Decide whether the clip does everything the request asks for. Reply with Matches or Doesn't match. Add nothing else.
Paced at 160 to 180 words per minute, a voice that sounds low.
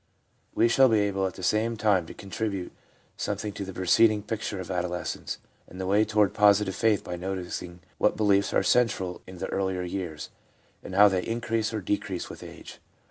Doesn't match